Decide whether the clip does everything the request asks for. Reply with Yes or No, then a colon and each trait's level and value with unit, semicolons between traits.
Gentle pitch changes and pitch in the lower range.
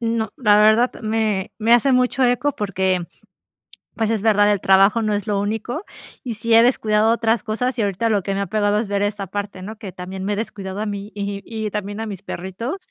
No: narrow, 2.2 semitones; high, 210 Hz